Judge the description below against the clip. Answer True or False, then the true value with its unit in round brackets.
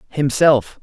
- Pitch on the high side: False (145 Hz)